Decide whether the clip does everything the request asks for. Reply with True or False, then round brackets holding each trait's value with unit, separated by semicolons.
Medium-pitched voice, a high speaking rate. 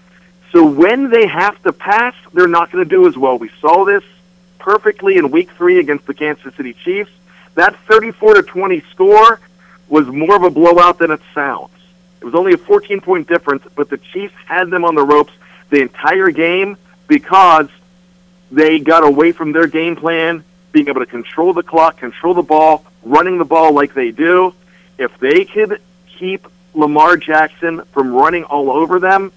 False (180 Hz; 185 wpm)